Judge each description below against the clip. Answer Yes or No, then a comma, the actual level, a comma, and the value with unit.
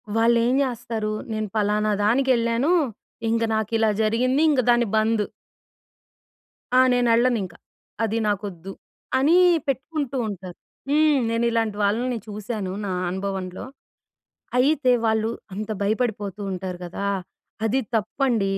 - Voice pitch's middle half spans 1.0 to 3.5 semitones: Yes, average, 3.2 semitones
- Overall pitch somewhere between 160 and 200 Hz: No, high, 225 Hz